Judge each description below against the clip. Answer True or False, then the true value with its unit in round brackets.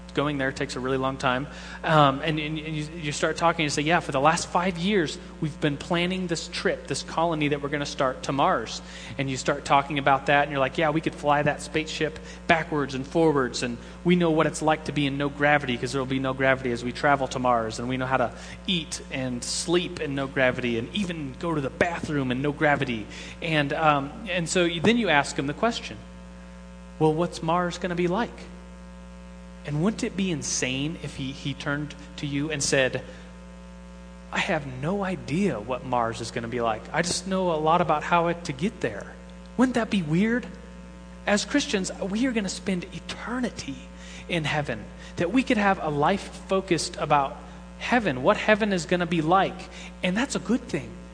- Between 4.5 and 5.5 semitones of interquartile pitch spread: True (5.2 semitones)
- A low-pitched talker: False (150 Hz)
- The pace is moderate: False (215 wpm)